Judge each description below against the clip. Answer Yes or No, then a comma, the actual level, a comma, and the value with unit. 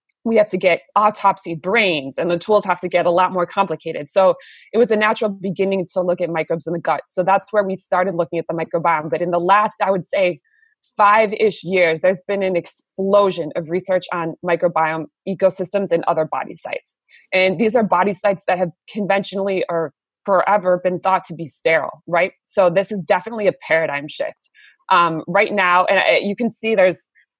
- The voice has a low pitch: No, medium, 185 Hz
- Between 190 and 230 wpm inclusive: Yes, average, 200 wpm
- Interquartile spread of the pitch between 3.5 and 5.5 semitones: No, average, 2.9 semitones